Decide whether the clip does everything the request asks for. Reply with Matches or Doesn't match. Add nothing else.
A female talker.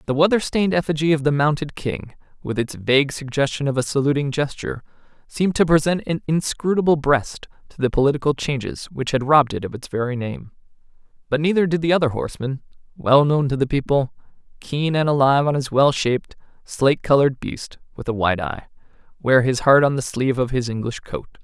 Doesn't match